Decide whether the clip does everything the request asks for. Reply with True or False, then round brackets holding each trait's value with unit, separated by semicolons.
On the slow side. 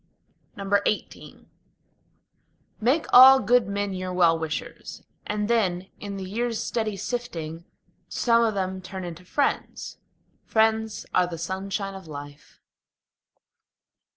True (115 wpm)